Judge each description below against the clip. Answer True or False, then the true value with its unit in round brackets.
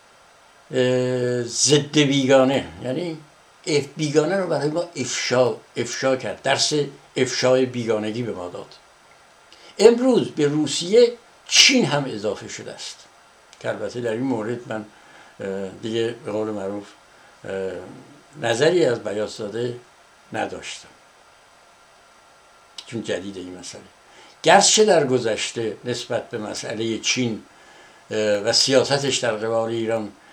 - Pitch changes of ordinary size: True (4.6 semitones)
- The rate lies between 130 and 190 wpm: False (110 wpm)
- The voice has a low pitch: True (125 Hz)